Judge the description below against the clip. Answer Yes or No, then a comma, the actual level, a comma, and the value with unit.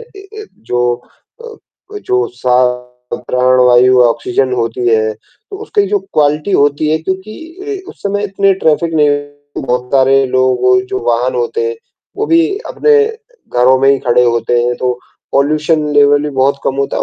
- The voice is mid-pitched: Yes, medium, 145 Hz